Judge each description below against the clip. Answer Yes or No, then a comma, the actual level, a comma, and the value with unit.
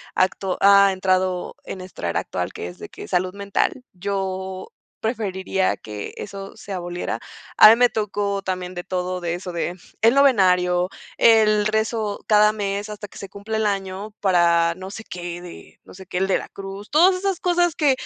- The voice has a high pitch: Yes, high, 195 Hz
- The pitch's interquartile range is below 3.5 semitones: Yes, average, 2.7 semitones